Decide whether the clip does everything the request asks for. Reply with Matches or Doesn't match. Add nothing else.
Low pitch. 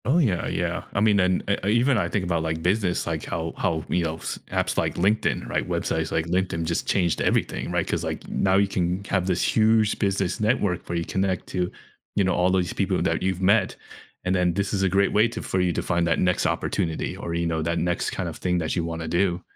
Matches